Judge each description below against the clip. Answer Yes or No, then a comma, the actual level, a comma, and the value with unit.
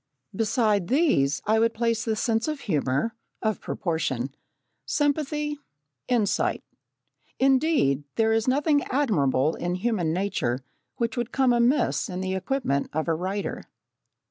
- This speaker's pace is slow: Yes, slow, 130 wpm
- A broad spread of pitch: Yes, wide, 7.2 semitones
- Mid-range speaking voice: No, high, 220 Hz